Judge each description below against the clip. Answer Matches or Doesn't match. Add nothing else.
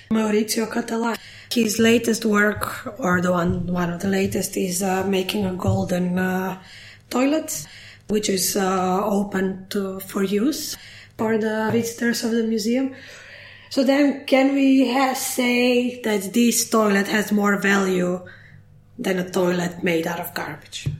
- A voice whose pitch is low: Doesn't match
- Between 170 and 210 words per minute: Doesn't match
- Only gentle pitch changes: Doesn't match